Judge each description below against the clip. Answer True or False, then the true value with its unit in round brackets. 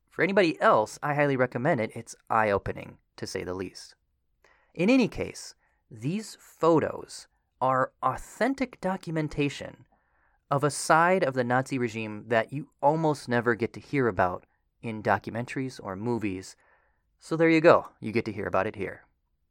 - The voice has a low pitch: True (125 Hz)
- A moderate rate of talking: True (160 wpm)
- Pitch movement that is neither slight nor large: False (5.7 semitones)